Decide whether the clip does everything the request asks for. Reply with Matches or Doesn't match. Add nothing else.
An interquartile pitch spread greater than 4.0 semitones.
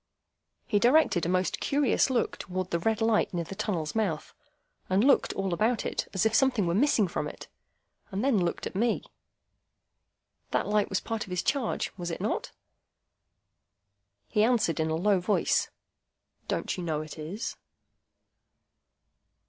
Matches